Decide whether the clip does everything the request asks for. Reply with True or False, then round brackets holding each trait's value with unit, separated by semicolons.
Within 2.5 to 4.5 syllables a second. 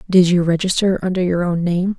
False (5.6 syllables/s)